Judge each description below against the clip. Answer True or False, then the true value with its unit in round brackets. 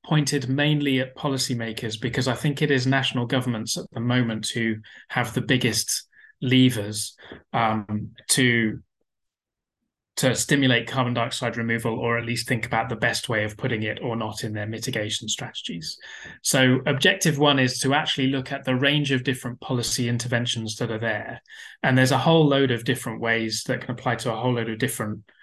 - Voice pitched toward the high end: False (125 Hz)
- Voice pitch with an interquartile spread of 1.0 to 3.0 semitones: True (2.6 semitones)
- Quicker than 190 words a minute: False (180 wpm)